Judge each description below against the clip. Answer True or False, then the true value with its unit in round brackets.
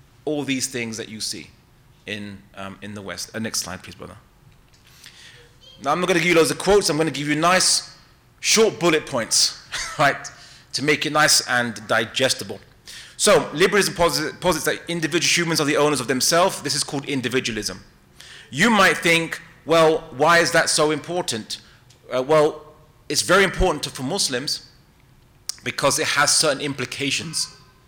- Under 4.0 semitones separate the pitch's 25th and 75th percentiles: False (4.9 semitones)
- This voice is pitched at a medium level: True (145 Hz)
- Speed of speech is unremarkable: True (170 wpm)